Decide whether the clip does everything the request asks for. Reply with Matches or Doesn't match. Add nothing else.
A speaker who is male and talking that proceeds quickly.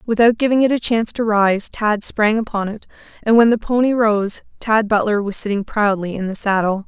Doesn't match